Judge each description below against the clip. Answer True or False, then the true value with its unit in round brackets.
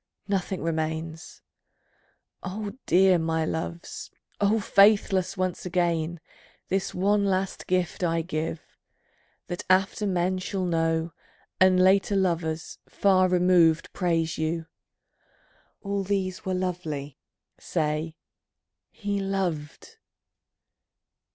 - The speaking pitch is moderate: True (180 Hz)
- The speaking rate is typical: False (100 wpm)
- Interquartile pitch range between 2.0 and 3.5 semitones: True (2.9 semitones)